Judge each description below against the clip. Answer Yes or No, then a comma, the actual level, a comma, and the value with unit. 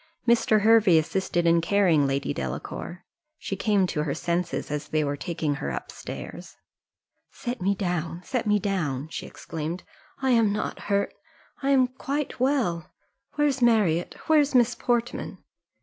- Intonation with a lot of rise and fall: Yes, wide, 6.4 semitones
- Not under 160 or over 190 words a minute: No, average, 150 wpm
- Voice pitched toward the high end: Yes, high, 195 Hz